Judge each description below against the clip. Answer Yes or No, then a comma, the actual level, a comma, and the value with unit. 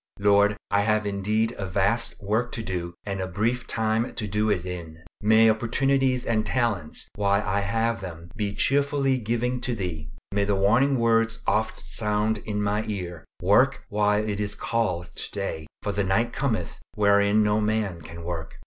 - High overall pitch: No, low, 105 Hz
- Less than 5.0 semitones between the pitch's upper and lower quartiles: Yes, narrow, 2.5 semitones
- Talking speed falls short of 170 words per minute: No, average, 175 wpm